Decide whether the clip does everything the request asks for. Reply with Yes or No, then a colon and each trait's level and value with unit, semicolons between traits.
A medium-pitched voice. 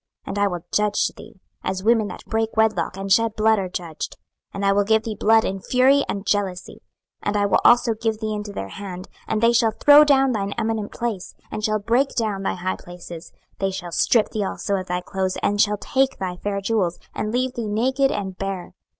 No: high, 210 Hz